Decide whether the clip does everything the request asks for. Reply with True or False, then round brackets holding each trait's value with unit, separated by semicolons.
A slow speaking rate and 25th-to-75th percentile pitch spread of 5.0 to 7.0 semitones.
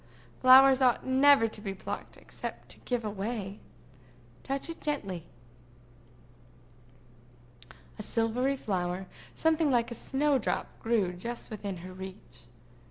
True (120 wpm; 5.5 semitones)